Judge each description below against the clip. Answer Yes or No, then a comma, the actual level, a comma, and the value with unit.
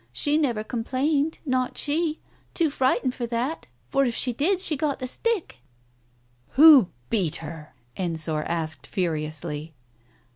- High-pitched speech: Yes, high, 240 Hz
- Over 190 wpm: No, average, 155 wpm